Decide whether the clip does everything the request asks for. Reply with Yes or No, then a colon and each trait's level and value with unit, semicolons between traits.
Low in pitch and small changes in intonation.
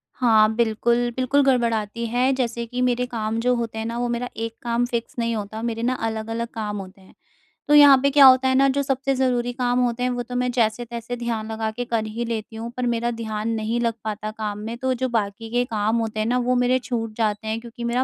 No: high, 235 Hz; narrow, 2.0 semitones